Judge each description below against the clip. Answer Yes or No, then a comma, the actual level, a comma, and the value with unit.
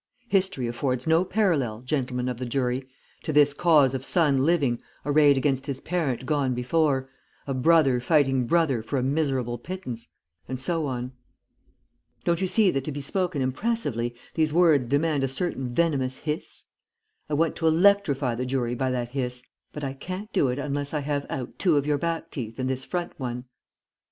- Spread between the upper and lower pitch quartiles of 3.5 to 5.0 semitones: Yes, average, 4.0 semitones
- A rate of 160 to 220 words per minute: Yes, average, 180 wpm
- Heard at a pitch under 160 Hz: Yes, medium, 140 Hz